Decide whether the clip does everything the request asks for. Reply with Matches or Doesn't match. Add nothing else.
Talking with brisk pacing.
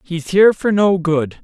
Matches